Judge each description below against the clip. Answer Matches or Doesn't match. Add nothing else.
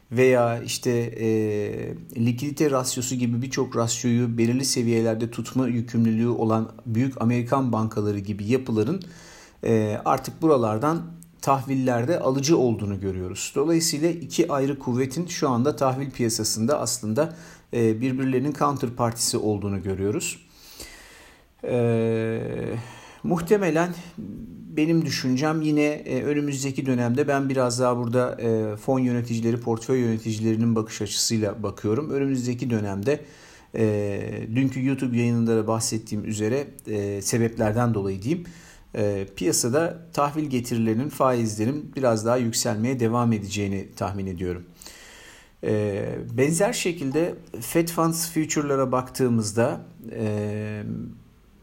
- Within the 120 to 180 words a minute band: Doesn't match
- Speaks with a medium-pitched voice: Doesn't match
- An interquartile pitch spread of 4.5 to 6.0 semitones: Doesn't match